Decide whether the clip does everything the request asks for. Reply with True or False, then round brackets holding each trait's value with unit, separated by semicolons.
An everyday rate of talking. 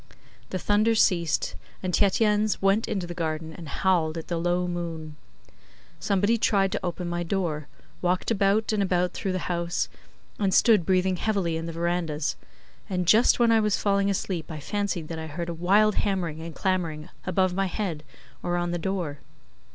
True (180 wpm)